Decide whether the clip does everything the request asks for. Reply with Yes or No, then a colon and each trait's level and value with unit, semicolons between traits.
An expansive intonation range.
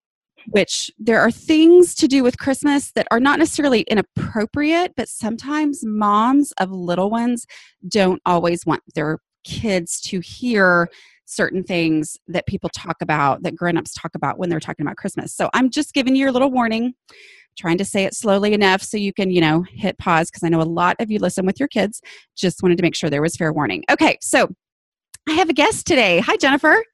Yes: wide, 7.4 semitones